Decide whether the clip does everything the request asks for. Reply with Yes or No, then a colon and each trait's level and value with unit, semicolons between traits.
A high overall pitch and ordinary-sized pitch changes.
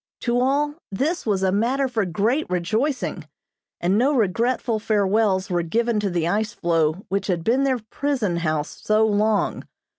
Yes: high, 215 Hz; average, 4.8 semitones